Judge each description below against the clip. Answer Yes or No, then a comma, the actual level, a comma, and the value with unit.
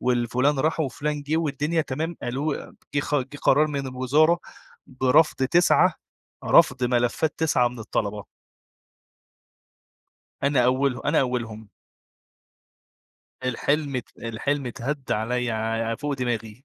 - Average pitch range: Yes, average, 3.4 semitones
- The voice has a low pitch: Yes, low, 130 Hz